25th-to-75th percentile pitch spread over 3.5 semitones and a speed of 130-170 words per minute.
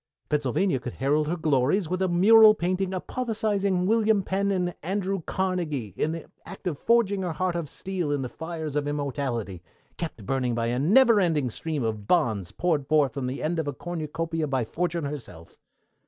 No: average, 5.2 semitones; average, 185 wpm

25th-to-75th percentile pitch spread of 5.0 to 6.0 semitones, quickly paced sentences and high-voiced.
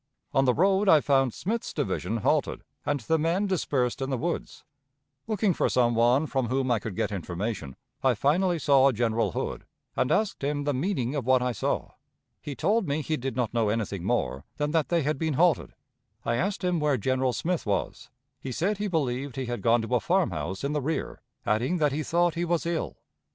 No: wide, 5.6 semitones; fast, 210 wpm; medium, 140 Hz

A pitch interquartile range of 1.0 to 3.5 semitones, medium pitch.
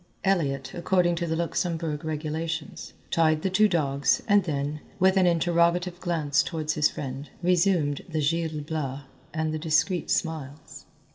Yes: narrow, 2.6 semitones; medium, 160 Hz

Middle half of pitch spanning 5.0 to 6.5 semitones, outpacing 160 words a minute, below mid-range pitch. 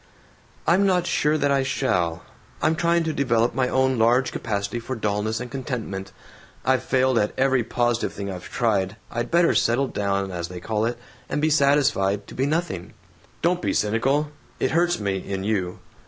Yes: wide, 5.6 semitones; average, 180 wpm; low, 120 Hz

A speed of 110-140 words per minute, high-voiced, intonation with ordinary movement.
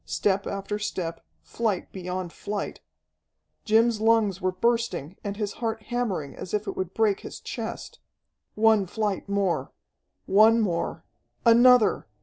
Yes: slow, 135 wpm; high, 205 Hz; average, 3.1 semitones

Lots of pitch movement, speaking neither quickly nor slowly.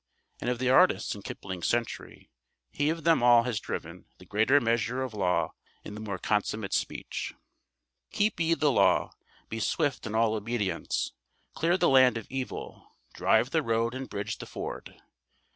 No: average, 3.8 semitones; average, 170 wpm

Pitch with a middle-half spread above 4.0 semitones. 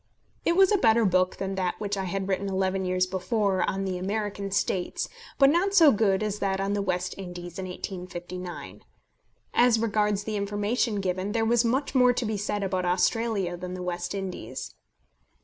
No: average, 3.0 semitones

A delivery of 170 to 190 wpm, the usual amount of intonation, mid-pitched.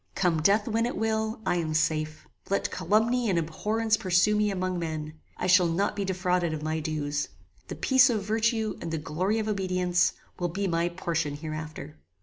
Yes: average, 185 wpm; average, 5.0 semitones; medium, 180 Hz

